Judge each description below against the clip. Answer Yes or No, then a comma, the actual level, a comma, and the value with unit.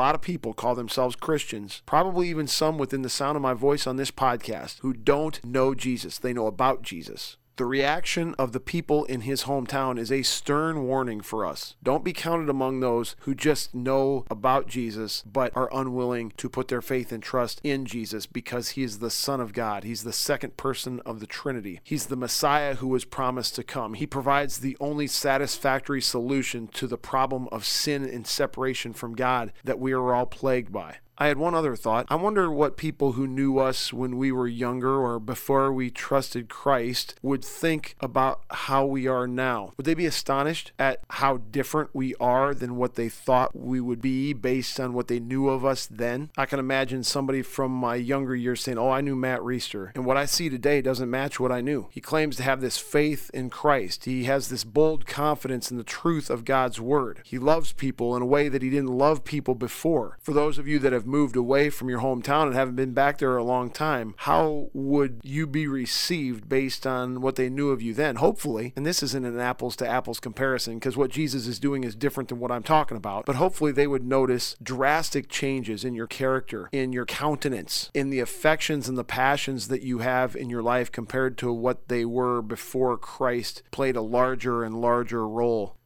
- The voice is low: Yes, low, 130 Hz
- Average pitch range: No, narrow, 2.1 semitones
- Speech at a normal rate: No, fast, 210 wpm